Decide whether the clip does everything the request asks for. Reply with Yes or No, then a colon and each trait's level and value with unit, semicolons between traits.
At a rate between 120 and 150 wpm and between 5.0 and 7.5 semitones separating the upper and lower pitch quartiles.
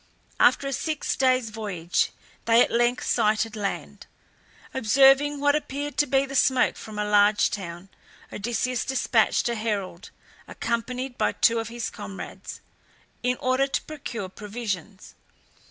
No: average, 140 wpm; average, 4.1 semitones